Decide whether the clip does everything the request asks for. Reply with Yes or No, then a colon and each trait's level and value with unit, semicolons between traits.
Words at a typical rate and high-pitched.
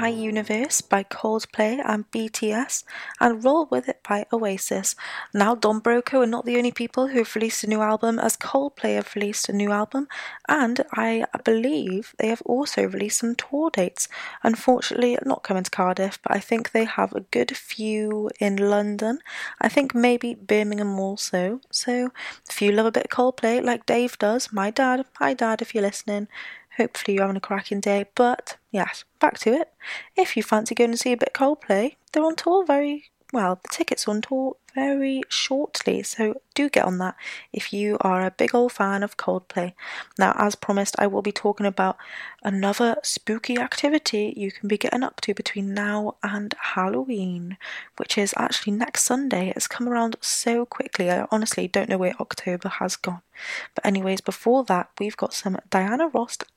Yes: average, 185 wpm; high, 220 Hz